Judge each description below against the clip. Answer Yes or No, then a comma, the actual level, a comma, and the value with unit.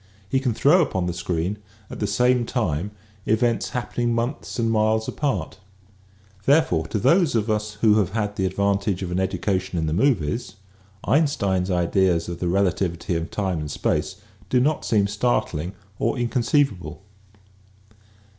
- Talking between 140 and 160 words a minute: Yes, average, 155 wpm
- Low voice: Yes, low, 105 Hz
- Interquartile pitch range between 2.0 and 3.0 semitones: No, average, 4.9 semitones